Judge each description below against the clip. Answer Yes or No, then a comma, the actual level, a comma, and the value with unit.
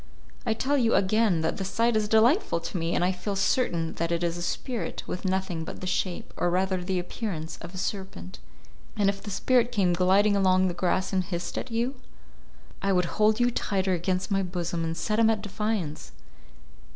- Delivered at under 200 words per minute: No, fast, 205 wpm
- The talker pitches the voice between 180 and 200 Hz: Yes, high, 190 Hz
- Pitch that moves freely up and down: No, average, 3.4 semitones